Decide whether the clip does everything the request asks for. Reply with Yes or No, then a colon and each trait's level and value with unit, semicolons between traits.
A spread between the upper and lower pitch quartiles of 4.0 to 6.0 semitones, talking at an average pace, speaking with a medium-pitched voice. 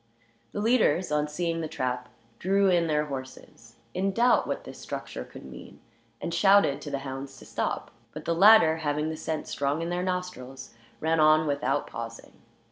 Yes: average, 4.3 semitones; average, 180 wpm; medium, 155 Hz